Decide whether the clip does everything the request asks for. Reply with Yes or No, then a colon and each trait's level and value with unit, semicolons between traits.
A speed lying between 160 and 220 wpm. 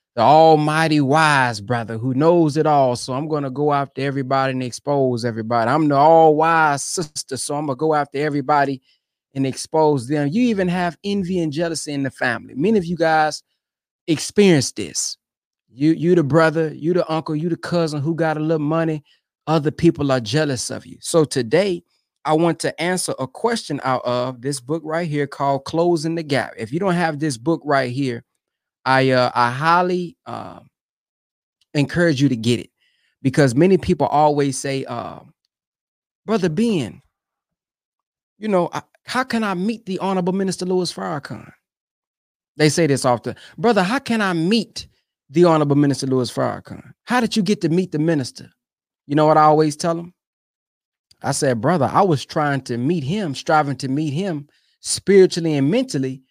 Yes: average, 180 wpm